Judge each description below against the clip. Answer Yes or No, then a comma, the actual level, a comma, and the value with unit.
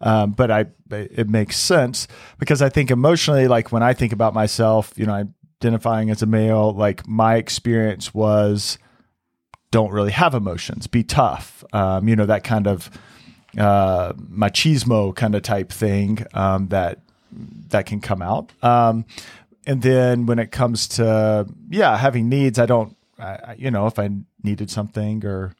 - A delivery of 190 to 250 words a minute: No, average, 165 wpm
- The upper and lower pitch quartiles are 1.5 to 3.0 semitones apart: Yes, narrow, 2.6 semitones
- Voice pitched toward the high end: No, low, 110 Hz